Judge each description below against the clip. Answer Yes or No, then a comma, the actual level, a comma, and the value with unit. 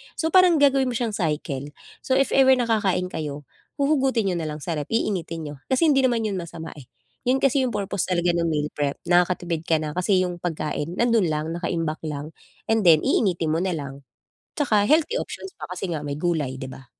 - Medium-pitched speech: Yes, medium, 175 Hz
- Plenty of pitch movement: Yes, wide, 7.3 semitones